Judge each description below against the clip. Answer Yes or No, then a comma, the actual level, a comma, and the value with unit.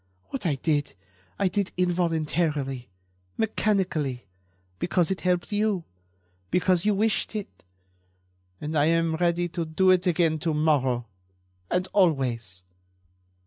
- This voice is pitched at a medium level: Yes, medium, 170 Hz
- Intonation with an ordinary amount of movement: Yes, average, 3.7 semitones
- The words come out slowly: Yes, slow, 120 wpm